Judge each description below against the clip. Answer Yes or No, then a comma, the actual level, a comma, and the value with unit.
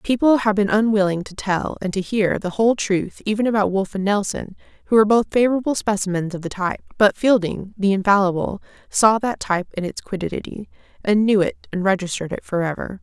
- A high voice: Yes, high, 200 Hz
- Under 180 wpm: No, average, 200 wpm